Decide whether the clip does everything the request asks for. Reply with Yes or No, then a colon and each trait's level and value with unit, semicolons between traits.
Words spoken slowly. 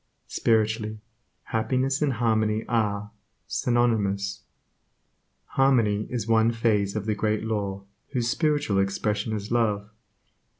Yes: slow, 110 wpm